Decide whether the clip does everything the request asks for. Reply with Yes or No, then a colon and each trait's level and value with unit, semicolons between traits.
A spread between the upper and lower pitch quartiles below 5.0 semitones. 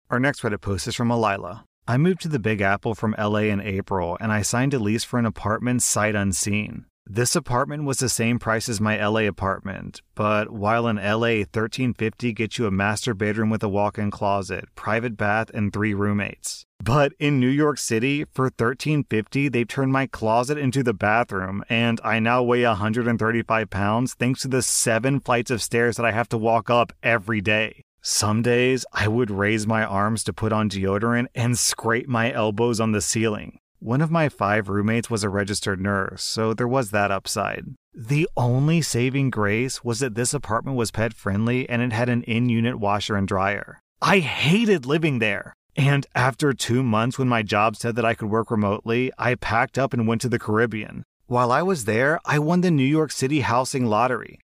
Yes: average, 2.9 semitones